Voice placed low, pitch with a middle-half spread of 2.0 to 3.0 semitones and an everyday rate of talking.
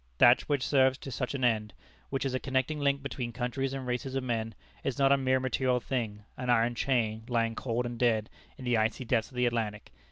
No: low, 125 Hz; narrow, 2.4 semitones; fast, 225 wpm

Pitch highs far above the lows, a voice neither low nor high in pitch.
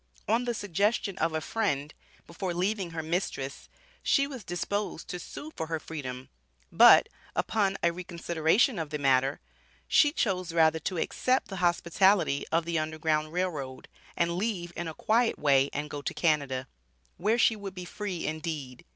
No: average, 4.3 semitones; medium, 170 Hz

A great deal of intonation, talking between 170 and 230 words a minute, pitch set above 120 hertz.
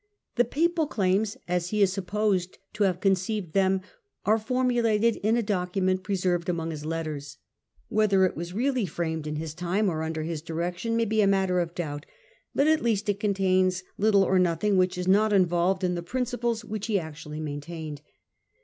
No: average, 3.8 semitones; average, 185 wpm; medium, 185 Hz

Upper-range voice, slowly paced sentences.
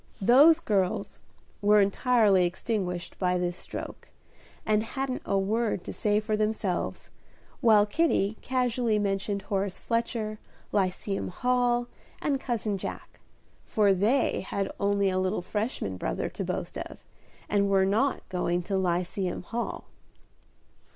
Yes: high, 205 Hz; slow, 130 wpm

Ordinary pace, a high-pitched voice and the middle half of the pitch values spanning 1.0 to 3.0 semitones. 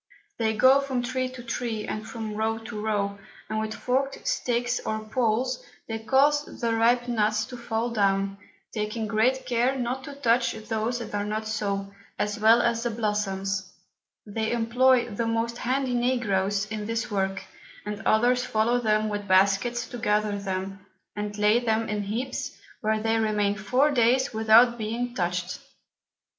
Yes: average, 165 wpm; high, 225 Hz; narrow, 2.6 semitones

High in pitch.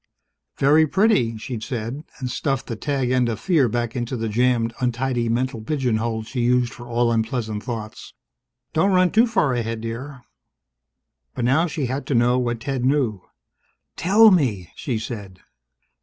No: low, 125 Hz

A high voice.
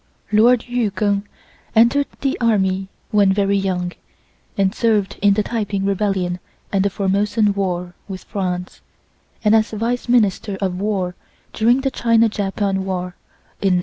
Yes: high, 200 Hz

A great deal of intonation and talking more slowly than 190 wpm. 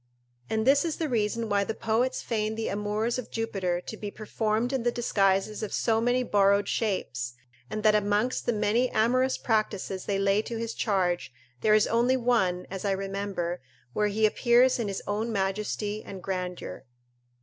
No: average, 2.8 semitones; average, 180 wpm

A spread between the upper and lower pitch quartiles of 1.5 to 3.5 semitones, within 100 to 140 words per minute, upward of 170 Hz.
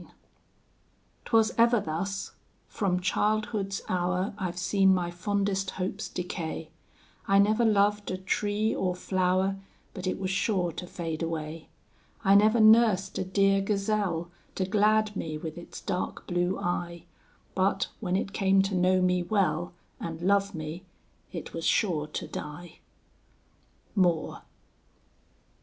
Yes: narrow, 2.4 semitones; slow, 135 wpm; high, 190 Hz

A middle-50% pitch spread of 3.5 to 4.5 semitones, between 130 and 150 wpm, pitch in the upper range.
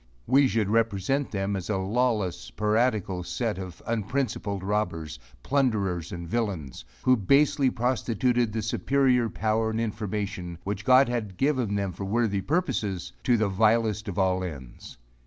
No: average, 4.0 semitones; average, 145 wpm; low, 105 Hz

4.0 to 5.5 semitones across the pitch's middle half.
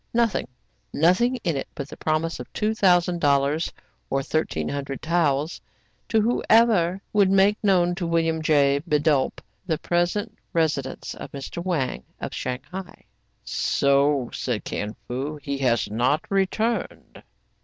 Yes: average, 5.0 semitones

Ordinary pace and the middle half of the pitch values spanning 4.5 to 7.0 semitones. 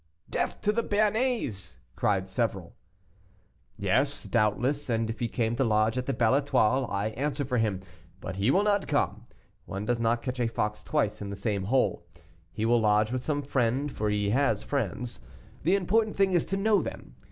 Yes: average, 190 wpm; average, 5.3 semitones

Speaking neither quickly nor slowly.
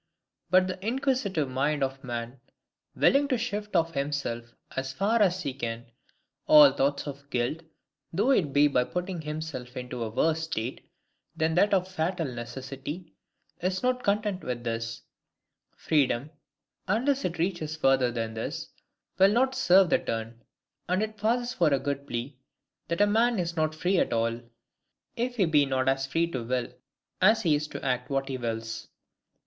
Yes: average, 170 wpm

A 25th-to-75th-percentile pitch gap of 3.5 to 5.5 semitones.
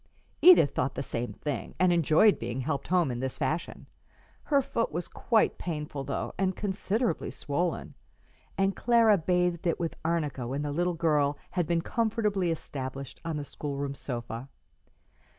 Yes: average, 4.9 semitones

